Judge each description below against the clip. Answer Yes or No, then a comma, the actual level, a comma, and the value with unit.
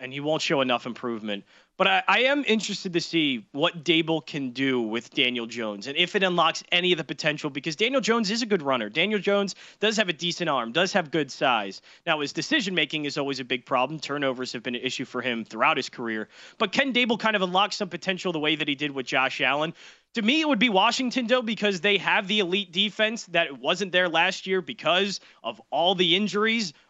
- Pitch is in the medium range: Yes, medium, 175 Hz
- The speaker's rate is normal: No, fast, 230 wpm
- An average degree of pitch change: No, wide, 6.7 semitones